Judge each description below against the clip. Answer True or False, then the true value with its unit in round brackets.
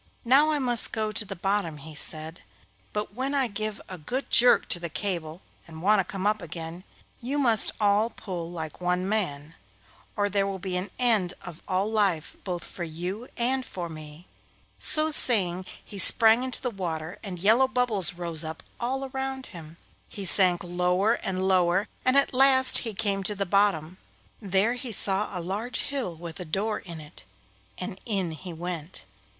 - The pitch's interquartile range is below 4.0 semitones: False (4.5 semitones)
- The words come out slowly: False (185 wpm)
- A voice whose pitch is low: False (195 Hz)